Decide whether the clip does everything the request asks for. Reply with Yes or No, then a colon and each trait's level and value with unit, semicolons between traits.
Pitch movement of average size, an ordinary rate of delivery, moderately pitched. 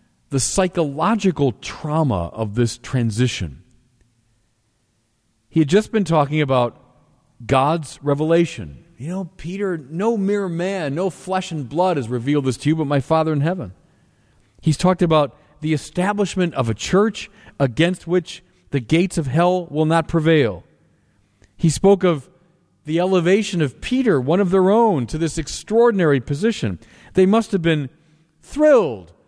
No: wide, 5.8 semitones; average, 145 wpm; medium, 160 Hz